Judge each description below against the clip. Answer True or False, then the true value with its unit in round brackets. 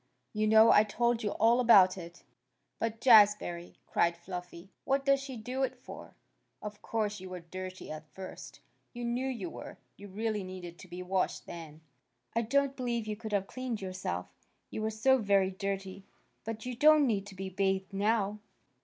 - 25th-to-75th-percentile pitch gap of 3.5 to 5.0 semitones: True (3.9 semitones)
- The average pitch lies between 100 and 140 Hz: False (205 Hz)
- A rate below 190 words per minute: True (180 wpm)